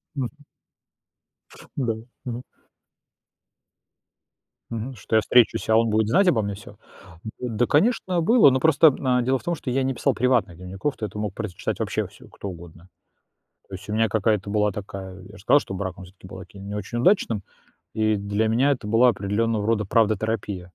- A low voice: Yes, low, 110 Hz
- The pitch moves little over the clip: No, average, 3.8 semitones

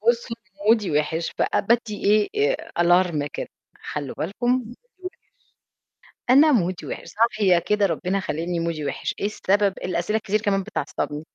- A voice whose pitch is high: Yes, high, 200 Hz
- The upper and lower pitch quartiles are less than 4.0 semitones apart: No, average, 4.5 semitones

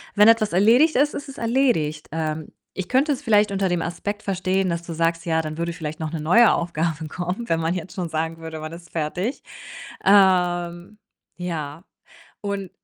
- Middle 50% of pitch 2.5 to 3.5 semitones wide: No, average, 3.9 semitones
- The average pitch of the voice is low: No, medium, 175 Hz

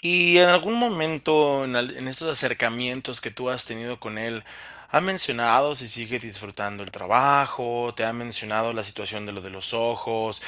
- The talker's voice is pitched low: Yes, low, 120 Hz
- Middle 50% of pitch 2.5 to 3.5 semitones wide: No, average, 4.1 semitones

